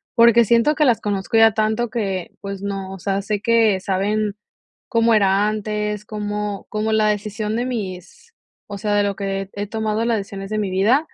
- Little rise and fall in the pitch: Yes, narrow, 2.0 semitones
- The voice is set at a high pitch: Yes, high, 210 Hz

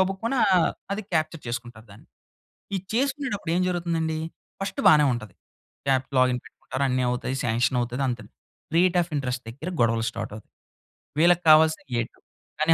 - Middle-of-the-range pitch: Yes, medium, 145 Hz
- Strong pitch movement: Yes, wide, 6.2 semitones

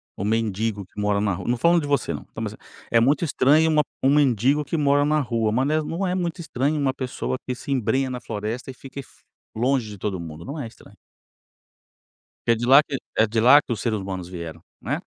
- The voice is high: No, low, 125 Hz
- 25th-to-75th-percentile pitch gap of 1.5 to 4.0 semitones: No, average, 5.1 semitones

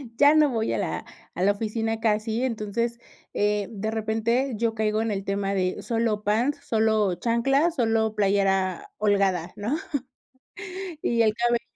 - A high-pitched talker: Yes, high, 220 Hz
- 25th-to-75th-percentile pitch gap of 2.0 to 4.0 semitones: Yes, narrow, 2.4 semitones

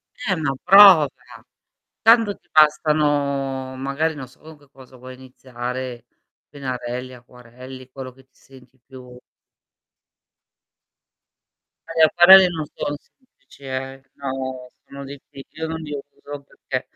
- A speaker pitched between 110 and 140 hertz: Yes, low, 135 Hz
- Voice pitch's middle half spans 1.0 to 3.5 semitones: Yes, average, 2.9 semitones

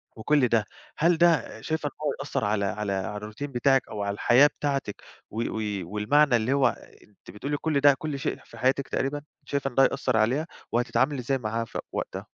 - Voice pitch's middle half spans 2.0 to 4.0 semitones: No, average, 5.0 semitones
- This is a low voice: Yes, low, 130 Hz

